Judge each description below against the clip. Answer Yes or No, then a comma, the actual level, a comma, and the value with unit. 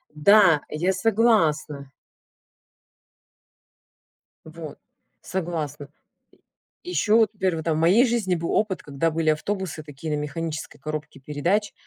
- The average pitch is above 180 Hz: No, medium, 165 Hz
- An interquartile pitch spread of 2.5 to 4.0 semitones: No, average, 4.7 semitones